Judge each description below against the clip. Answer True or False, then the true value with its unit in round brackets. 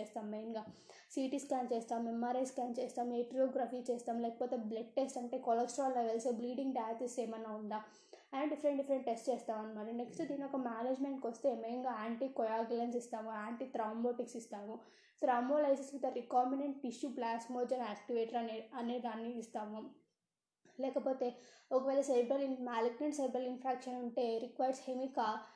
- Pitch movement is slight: True (2.3 semitones)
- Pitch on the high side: True (245 Hz)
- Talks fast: True (130 wpm)